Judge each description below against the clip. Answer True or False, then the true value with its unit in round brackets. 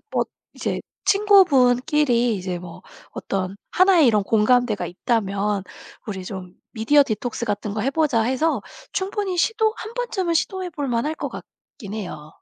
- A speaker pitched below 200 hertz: False (245 Hz)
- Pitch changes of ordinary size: False (8.2 semitones)